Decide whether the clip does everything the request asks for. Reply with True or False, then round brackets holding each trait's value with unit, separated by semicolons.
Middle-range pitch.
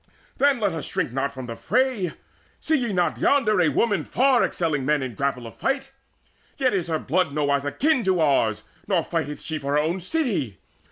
True (165 Hz)